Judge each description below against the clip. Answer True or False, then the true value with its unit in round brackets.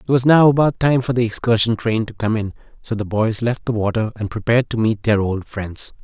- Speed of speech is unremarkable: False (250 wpm)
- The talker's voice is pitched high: False (115 Hz)